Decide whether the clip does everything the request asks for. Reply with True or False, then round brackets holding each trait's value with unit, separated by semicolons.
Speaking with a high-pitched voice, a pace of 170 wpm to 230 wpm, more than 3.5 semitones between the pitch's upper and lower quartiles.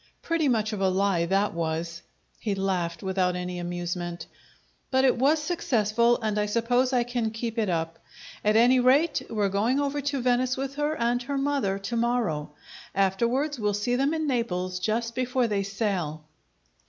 True (225 Hz; 175 wpm; 5.1 semitones)